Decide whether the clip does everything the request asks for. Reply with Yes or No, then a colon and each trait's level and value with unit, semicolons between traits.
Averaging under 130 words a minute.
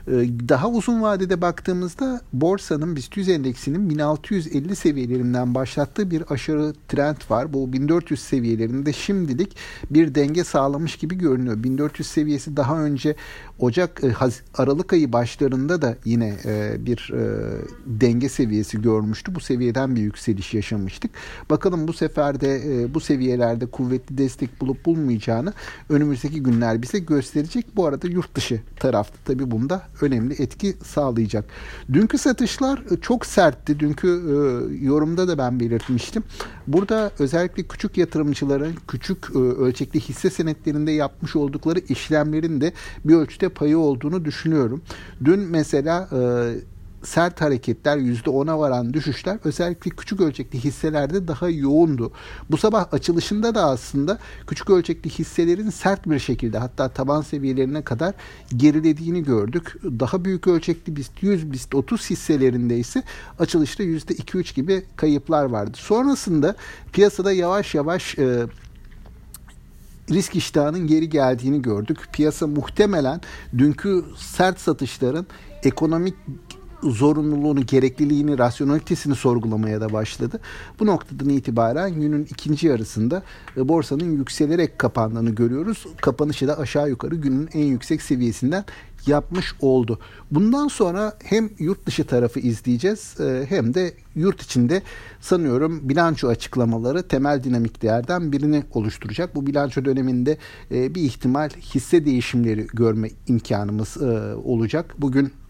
Yes: average, 120 wpm